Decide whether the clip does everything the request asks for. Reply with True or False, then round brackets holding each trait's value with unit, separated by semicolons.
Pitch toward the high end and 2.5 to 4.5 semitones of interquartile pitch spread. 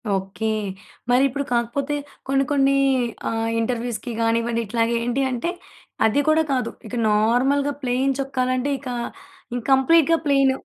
True (255 Hz; 2.9 semitones)